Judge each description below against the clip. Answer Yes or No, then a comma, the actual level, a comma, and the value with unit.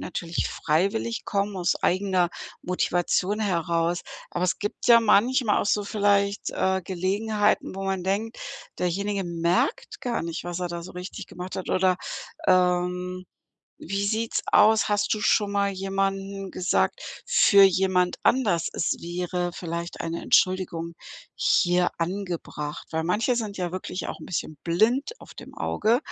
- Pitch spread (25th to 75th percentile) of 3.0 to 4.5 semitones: No, narrow, 2.6 semitones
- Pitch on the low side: No, medium, 185 Hz